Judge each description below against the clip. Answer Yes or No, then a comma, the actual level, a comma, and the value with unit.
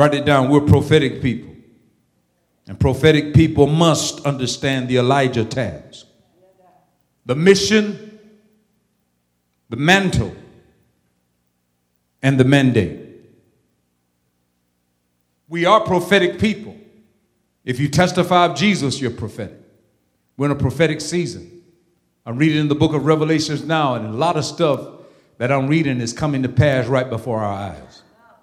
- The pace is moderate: No, slow, 130 wpm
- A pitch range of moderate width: No, wide, 8.7 semitones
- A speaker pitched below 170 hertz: Yes, medium, 140 Hz